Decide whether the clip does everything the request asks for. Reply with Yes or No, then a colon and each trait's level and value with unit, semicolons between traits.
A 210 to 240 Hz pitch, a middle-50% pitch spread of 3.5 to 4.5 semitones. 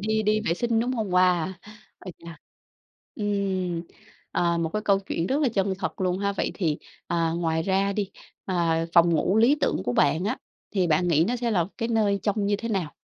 No: high, 190 Hz; average, 3.9 semitones